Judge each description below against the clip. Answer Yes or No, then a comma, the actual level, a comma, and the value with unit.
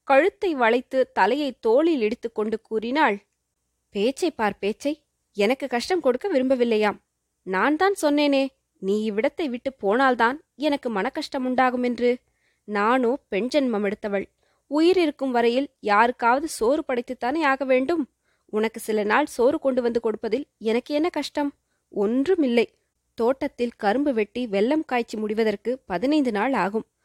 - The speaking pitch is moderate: No, high, 245 Hz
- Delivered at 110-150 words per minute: Yes, average, 125 wpm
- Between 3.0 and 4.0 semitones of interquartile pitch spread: No, average, 4.6 semitones